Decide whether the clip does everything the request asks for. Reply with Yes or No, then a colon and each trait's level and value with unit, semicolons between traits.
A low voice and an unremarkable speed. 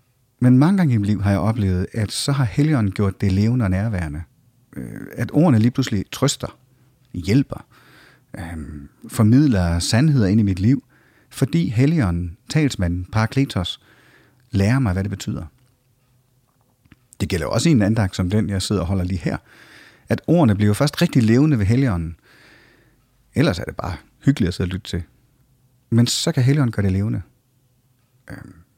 Yes: low, 115 Hz; average, 165 wpm